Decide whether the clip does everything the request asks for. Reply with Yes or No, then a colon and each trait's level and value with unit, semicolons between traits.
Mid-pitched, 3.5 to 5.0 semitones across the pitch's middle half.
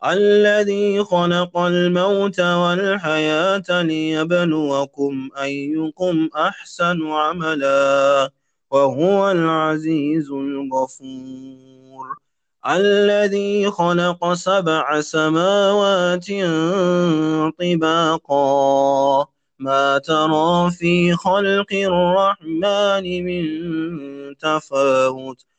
Yes: medium, 160 Hz; average, 4.6 semitones